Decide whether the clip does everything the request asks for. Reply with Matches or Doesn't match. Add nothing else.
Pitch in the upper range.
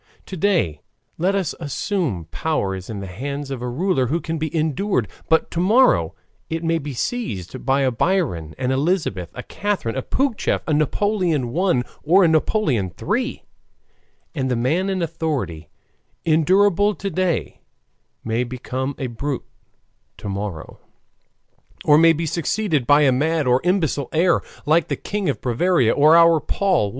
Doesn't match